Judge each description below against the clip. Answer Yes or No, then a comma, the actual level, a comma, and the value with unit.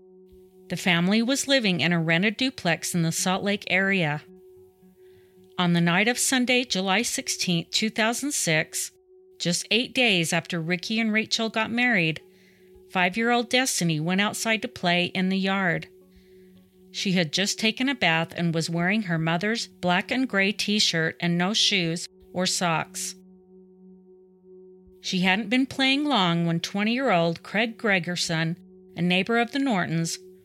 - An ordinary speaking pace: Yes, average, 155 wpm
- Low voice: No, medium, 185 Hz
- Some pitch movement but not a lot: Yes, average, 3.7 semitones